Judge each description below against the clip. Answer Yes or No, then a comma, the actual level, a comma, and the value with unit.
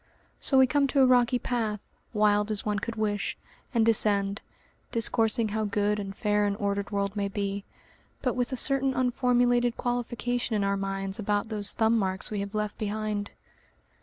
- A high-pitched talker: Yes, high, 215 Hz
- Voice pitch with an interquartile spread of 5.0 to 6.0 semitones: No, average, 3.0 semitones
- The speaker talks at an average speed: Yes, average, 175 wpm